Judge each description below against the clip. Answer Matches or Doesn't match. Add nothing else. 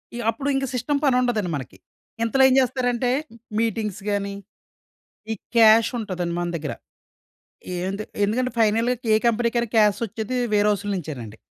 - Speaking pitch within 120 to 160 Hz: Doesn't match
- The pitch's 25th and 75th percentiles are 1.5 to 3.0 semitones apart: Doesn't match